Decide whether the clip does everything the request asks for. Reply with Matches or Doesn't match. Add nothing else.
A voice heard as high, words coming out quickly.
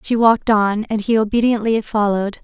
Doesn't match